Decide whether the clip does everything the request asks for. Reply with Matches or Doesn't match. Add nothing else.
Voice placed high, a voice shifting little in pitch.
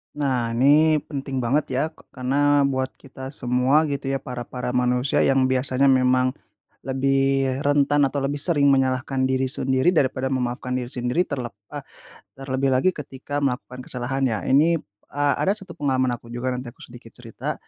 Doesn't match